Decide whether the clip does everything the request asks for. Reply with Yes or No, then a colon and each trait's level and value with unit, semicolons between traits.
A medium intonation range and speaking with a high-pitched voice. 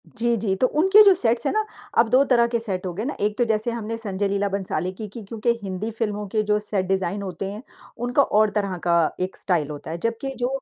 Yes: average, 3.6 semitones; high, 210 Hz